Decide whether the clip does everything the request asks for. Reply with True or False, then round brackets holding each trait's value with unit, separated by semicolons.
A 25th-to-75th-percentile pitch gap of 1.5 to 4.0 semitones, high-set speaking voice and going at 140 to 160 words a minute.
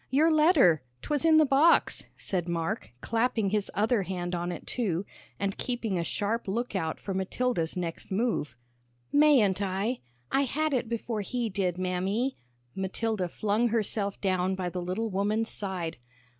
False (4.6 semitones; 205 Hz; 155 wpm)